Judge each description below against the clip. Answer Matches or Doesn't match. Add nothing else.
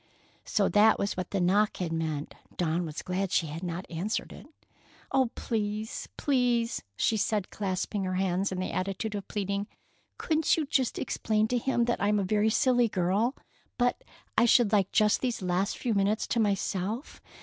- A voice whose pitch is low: Doesn't match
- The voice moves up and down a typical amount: Matches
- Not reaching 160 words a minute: Doesn't match